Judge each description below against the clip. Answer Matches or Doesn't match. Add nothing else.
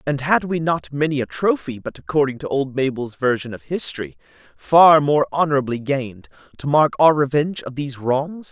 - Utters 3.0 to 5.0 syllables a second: Doesn't match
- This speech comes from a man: Matches